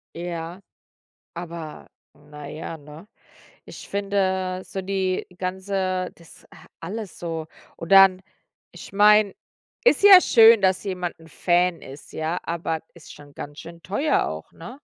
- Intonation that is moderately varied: Yes, average, 3.0 semitones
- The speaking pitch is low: No, medium, 185 Hz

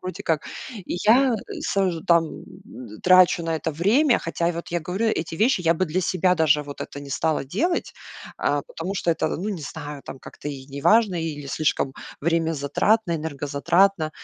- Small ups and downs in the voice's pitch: No, average, 3.9 semitones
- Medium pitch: Yes, medium, 165 Hz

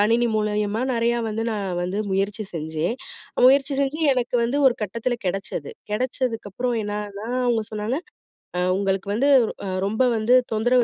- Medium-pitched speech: No, high, 220 Hz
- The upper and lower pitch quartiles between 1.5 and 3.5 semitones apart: Yes, average, 3.2 semitones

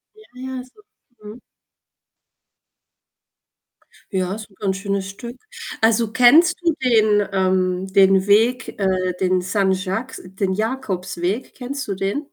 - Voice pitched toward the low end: No, high, 200 Hz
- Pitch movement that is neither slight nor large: Yes, average, 4.3 semitones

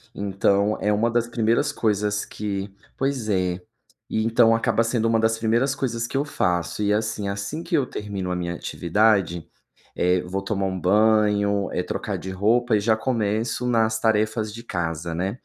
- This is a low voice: Yes, low, 105 Hz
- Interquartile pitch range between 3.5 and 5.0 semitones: No, average, 2.7 semitones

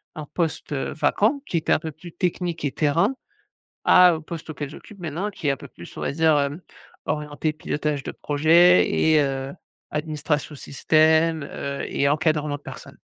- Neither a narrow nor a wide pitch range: No, narrow, 2.3 semitones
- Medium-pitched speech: Yes, medium, 155 Hz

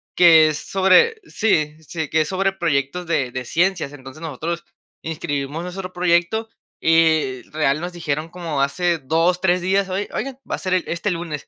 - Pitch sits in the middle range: Yes, medium, 165 Hz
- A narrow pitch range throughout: No, average, 3.2 semitones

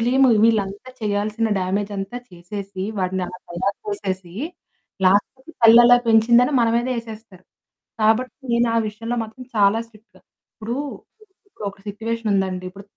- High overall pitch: Yes, high, 215 Hz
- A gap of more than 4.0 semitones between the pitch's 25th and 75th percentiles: No, average, 3.1 semitones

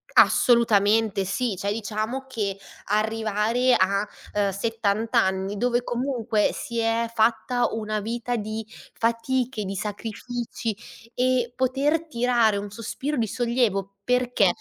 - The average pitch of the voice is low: No, high, 225 Hz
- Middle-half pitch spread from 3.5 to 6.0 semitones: No, average, 2.8 semitones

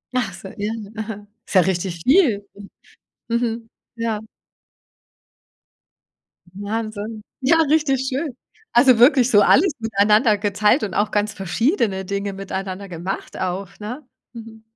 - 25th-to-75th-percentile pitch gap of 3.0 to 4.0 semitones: Yes, average, 3.3 semitones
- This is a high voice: Yes, high, 215 Hz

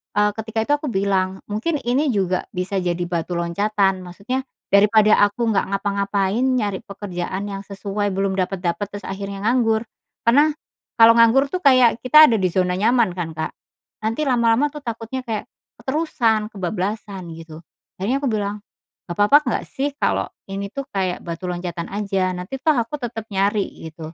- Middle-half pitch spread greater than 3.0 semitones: Yes, average, 3.8 semitones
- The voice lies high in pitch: Yes, high, 205 Hz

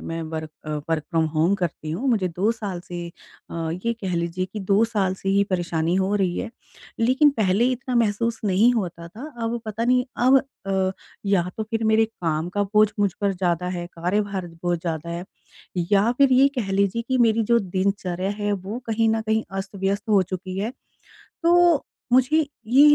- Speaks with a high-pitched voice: Yes, high, 200 Hz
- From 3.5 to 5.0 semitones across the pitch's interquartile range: Yes, average, 4.0 semitones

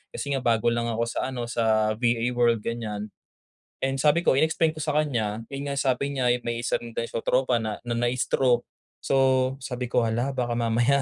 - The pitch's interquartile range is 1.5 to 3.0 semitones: Yes, narrow, 2.4 semitones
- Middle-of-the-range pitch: No, low, 120 Hz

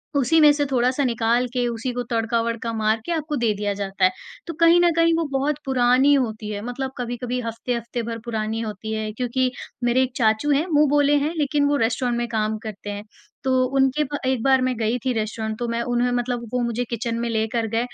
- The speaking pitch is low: No, high, 240 Hz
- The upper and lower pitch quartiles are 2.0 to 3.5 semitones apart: Yes, average, 2.9 semitones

